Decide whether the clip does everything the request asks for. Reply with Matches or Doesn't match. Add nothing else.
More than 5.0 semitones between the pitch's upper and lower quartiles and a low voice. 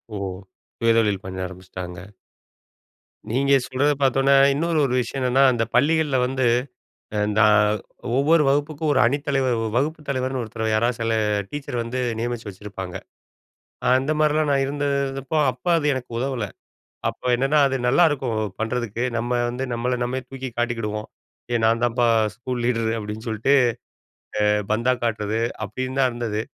Doesn't match